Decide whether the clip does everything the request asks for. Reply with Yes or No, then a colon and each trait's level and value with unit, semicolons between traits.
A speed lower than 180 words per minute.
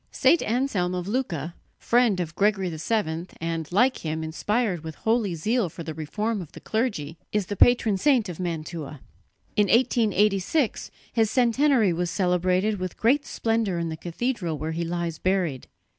Yes: average, 160 wpm